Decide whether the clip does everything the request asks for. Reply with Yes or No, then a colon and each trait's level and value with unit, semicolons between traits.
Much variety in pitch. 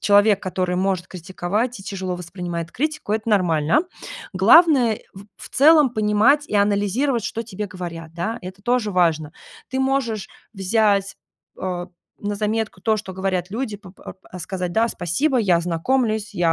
No: average, 3.8 semitones